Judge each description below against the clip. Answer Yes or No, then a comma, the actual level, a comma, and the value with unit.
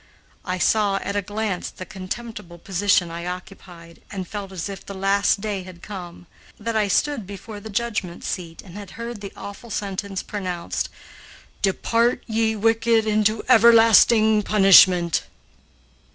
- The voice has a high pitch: Yes, high, 200 Hz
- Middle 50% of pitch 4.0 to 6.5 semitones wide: No, average, 2.9 semitones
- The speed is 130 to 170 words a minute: Yes, average, 145 wpm